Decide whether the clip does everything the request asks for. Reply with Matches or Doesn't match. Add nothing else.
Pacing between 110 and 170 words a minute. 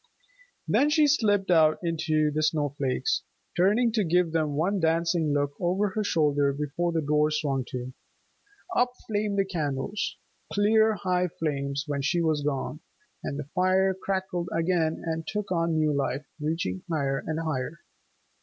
Matches